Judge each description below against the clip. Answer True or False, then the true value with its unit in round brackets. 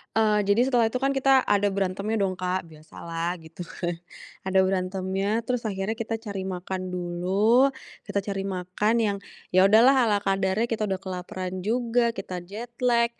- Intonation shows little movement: False (3.4 semitones)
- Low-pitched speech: False (195 Hz)